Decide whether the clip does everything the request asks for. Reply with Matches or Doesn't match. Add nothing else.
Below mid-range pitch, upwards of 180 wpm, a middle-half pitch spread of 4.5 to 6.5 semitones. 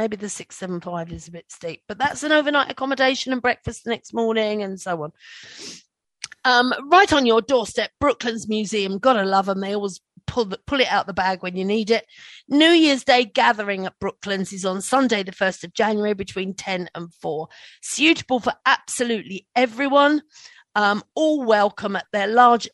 Doesn't match